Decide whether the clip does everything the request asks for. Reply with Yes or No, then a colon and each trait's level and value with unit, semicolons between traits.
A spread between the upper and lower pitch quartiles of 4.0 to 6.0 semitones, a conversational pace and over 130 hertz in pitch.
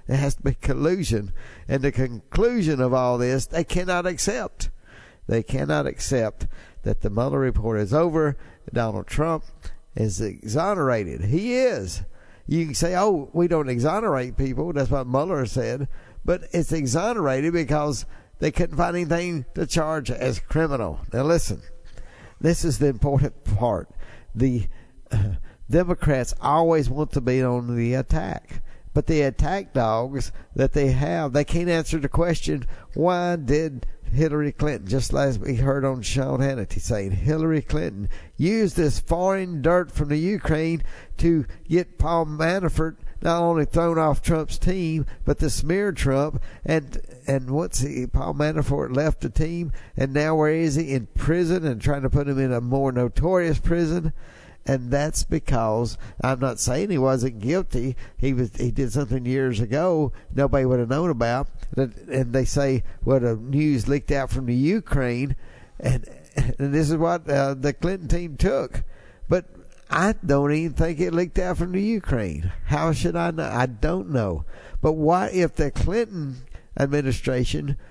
Yes: average, 4.6 semitones; average, 160 wpm; medium, 140 Hz